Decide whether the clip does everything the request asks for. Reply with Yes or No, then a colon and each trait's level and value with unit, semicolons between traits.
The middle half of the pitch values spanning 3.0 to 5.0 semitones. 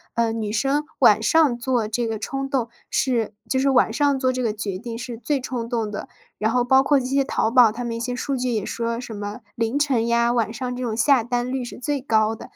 No: narrow, 2.6 semitones